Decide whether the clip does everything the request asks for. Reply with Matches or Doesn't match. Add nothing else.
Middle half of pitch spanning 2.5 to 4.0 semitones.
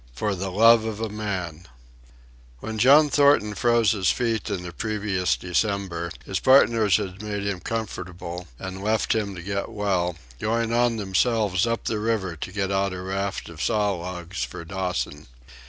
Matches